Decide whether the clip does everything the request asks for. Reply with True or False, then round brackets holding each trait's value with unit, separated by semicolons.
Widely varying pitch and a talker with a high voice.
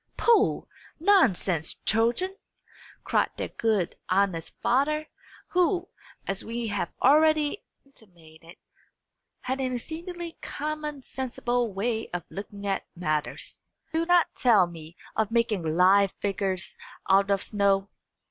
True (7.8 semitones; 225 Hz)